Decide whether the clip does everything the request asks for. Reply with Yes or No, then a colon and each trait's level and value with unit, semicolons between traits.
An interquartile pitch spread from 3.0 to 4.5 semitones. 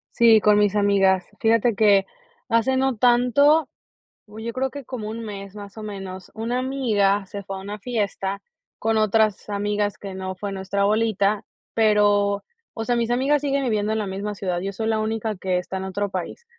No: narrow, 2.5 semitones